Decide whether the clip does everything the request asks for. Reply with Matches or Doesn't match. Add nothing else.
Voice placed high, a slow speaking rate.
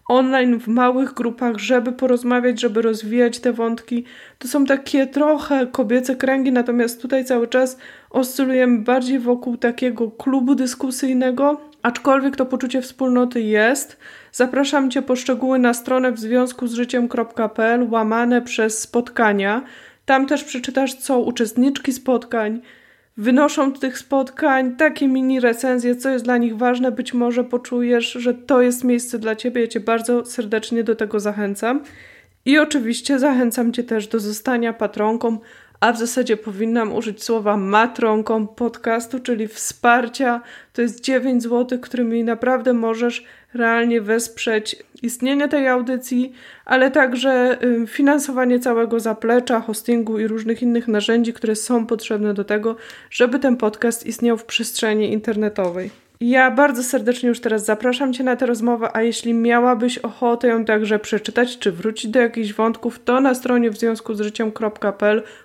Doesn't match